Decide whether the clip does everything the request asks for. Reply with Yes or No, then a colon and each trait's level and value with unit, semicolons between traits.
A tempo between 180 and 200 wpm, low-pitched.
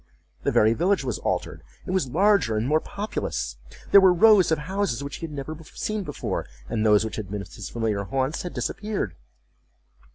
No: average, 190 wpm; medium, 150 Hz